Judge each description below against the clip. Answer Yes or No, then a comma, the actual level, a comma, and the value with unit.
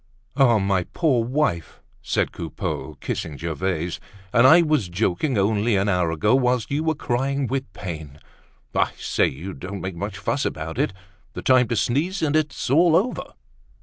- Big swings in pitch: Yes, wide, 7.3 semitones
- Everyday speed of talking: Yes, average, 165 wpm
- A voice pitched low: Yes, low, 110 Hz